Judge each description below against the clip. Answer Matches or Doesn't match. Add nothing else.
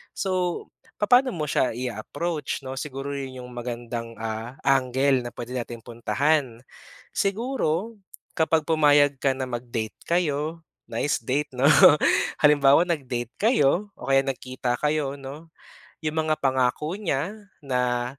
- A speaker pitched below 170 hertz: Matches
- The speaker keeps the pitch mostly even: Doesn't match